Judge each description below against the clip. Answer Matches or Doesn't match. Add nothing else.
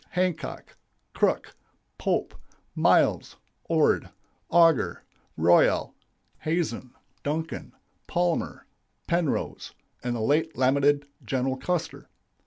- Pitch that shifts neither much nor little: Matches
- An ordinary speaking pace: Doesn't match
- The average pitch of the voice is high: Doesn't match